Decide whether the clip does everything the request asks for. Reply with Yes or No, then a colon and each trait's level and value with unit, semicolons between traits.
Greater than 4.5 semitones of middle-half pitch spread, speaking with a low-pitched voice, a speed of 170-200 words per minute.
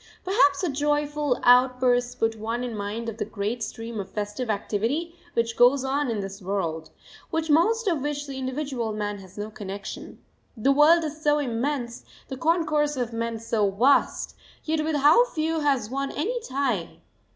No: average, 5.2 semitones; very high, 255 Hz; average, 175 wpm